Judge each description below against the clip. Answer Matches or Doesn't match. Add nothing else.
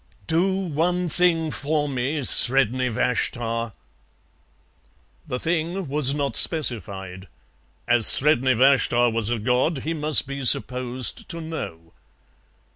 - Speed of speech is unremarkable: Doesn't match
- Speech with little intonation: Doesn't match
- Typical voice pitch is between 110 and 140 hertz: Matches